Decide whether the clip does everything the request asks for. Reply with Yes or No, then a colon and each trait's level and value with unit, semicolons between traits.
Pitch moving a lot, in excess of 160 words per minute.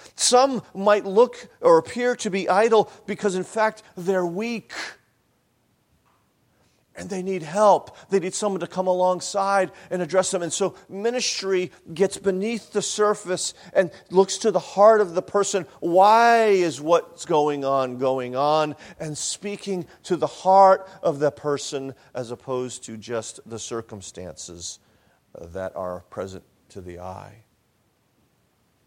No: wide, 6.8 semitones; average, 140 wpm